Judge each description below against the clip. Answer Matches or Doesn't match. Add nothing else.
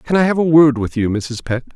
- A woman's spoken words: Doesn't match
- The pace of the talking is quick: Matches